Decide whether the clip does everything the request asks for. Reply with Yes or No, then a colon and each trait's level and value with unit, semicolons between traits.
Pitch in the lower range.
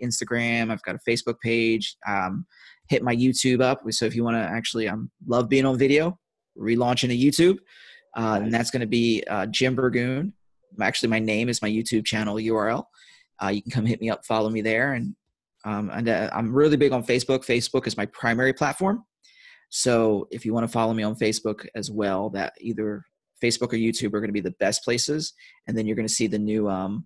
Yes: low, 115 Hz